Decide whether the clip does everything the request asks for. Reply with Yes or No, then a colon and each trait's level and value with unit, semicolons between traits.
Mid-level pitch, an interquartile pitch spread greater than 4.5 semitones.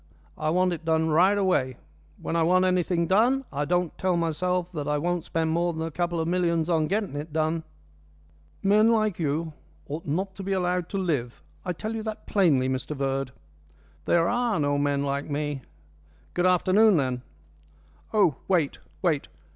No: medium, 170 Hz; average, 3.6 semitones